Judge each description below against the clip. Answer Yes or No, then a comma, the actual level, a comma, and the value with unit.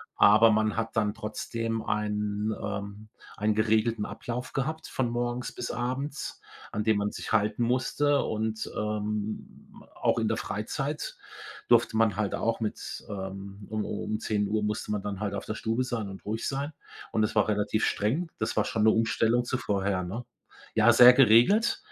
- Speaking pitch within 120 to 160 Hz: No, low, 110 Hz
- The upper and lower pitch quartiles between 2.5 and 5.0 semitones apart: No, narrow, 2.1 semitones